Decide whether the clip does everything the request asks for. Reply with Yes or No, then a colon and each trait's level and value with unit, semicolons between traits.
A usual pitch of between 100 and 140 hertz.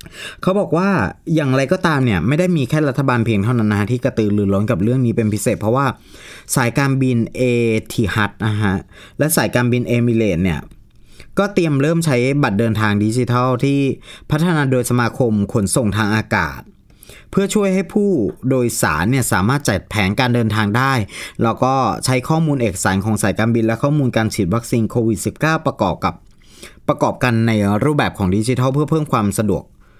Yes: low, 120 Hz